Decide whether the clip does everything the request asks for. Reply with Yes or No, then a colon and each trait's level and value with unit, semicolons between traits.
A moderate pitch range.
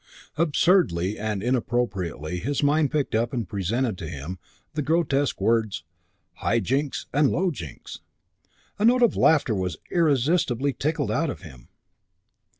No: wide, 7.8 semitones